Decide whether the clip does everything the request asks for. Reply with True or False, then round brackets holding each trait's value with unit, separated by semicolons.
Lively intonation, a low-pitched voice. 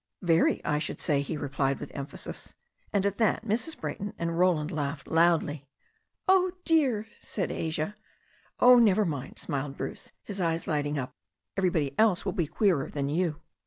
False (5.7 semitones; 165 Hz)